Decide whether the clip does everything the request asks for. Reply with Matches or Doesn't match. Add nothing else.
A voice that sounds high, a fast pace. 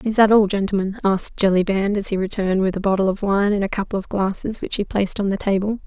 Matches